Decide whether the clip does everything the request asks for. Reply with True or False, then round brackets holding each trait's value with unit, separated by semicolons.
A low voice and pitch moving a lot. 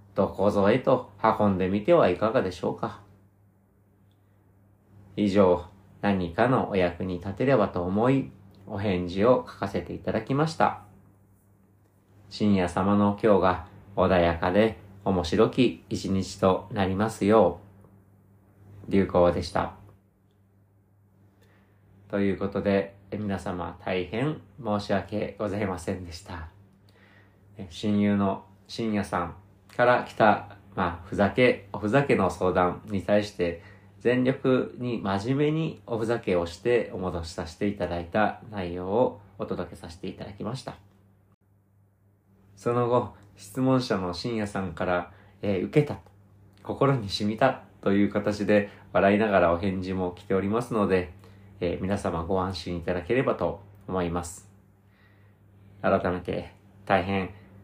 False (100 Hz; 1.4 semitones)